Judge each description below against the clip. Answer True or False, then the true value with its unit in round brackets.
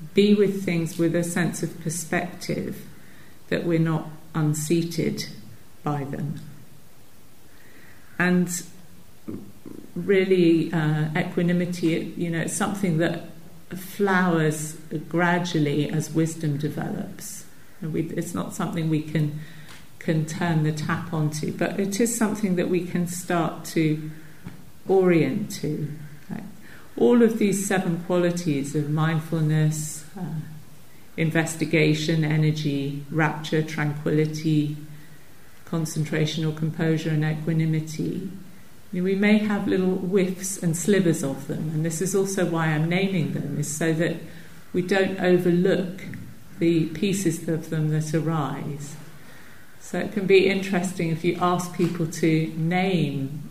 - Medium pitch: True (165 Hz)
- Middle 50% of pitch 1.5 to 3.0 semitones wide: True (2.5 semitones)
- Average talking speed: False (120 wpm)